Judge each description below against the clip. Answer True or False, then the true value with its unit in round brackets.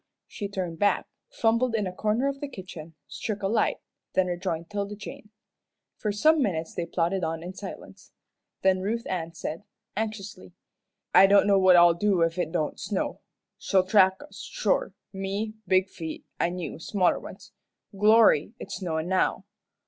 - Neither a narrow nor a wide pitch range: True (3.3 semitones)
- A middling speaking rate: True (165 wpm)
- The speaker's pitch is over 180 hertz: True (190 Hz)